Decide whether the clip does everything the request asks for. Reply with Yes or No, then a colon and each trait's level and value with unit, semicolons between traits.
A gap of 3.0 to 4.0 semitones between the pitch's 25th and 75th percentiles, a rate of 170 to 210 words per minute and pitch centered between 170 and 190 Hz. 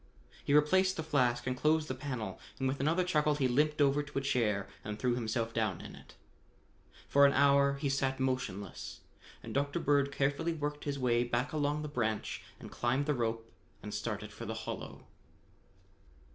No: average, 3.4 semitones; average, 185 wpm; medium, 140 Hz